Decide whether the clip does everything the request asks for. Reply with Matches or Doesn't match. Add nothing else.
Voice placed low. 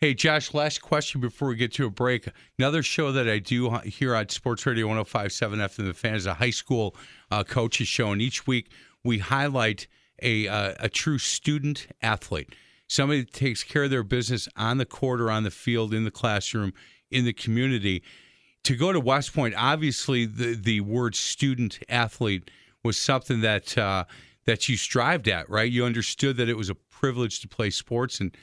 Matches